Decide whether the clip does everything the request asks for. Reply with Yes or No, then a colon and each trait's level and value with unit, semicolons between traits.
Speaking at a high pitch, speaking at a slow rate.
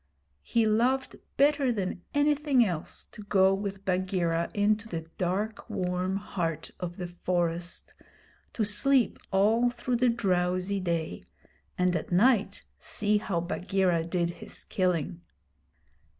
Yes: high, 195 Hz; slow, 125 wpm